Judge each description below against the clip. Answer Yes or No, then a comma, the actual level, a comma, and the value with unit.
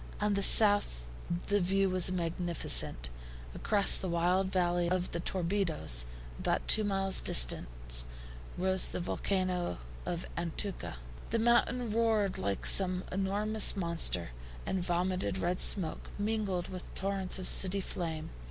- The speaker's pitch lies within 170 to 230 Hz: Yes, medium, 185 Hz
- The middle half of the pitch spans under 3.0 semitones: Yes, narrow, 2.4 semitones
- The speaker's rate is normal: No, slow, 130 wpm